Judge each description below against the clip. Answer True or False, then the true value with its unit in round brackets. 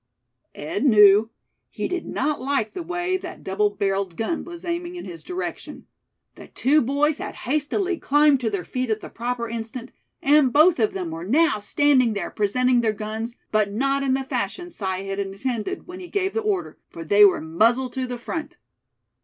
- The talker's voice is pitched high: True (250 Hz)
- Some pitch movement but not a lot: False (6.6 semitones)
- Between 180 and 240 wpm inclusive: True (190 wpm)